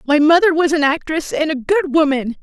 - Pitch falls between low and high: No, very high, 305 Hz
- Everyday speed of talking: No, fast, 220 wpm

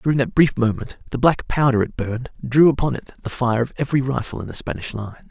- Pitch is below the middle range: Yes, low, 130 Hz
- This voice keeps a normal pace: No, fast, 235 wpm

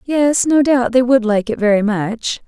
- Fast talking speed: Yes, fast, 220 wpm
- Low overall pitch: No, high, 240 Hz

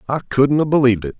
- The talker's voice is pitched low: Yes, low, 130 Hz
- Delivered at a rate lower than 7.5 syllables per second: No, 7.7 syllables/s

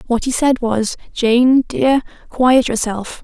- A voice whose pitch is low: No, high, 245 Hz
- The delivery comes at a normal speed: Yes, average, 150 wpm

